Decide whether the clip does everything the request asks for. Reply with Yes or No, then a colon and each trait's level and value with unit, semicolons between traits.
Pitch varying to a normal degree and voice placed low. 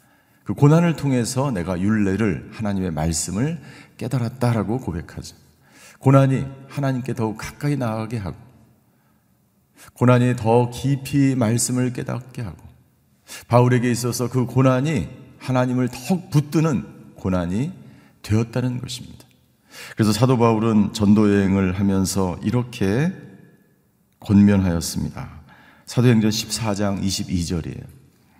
Yes: average, 4.3 semitones; low, 120 Hz